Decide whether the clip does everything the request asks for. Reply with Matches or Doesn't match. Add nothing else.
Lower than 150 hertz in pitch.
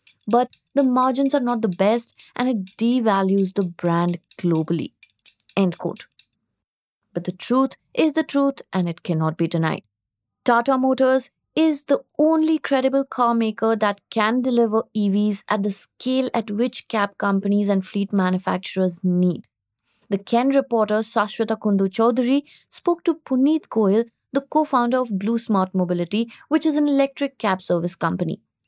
Doesn't match